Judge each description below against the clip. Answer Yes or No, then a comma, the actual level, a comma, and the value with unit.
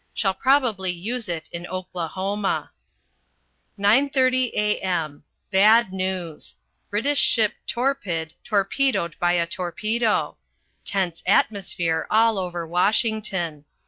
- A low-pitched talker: No, high, 195 Hz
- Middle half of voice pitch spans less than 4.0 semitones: No, average, 4.4 semitones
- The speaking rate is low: Yes, slow, 95 wpm